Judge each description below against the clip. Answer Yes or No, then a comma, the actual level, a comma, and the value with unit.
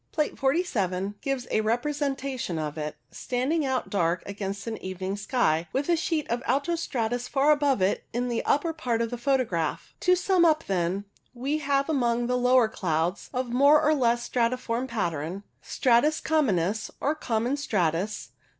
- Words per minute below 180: Yes, average, 170 wpm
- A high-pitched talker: Yes, high, 245 Hz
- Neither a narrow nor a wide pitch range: No, wide, 6.0 semitones